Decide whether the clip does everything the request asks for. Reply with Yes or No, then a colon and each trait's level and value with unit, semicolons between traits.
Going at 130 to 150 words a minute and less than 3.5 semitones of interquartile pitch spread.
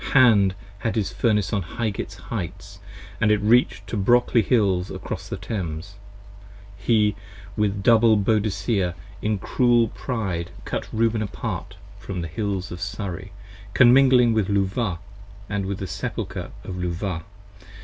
Yes: average, 140 wpm; average, 3.1 semitones